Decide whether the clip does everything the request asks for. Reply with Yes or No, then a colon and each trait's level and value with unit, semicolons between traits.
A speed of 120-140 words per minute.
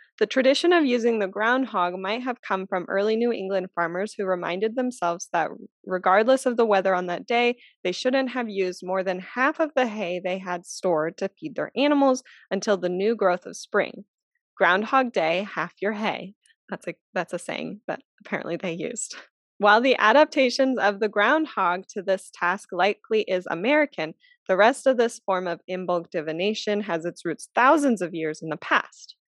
No: average, 185 wpm